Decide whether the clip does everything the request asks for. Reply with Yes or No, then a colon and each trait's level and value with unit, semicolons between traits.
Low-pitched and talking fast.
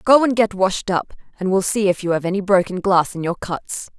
No: high, 190 Hz; fast, 255 wpm